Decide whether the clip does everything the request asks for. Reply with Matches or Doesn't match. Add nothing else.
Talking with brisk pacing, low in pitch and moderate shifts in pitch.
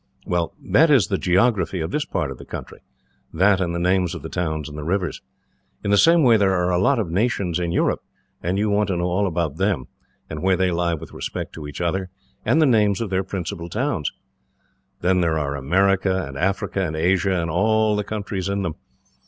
Matches